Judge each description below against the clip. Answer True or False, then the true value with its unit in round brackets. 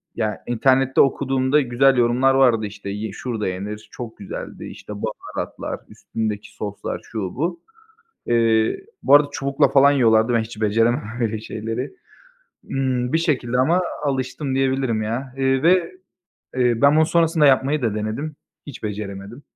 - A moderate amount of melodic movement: True (3.8 semitones)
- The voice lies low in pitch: True (125 Hz)